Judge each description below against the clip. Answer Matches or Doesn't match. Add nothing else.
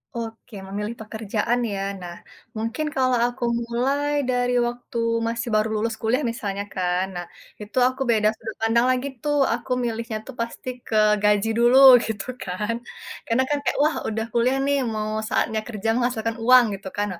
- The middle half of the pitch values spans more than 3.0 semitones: Doesn't match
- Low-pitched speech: Doesn't match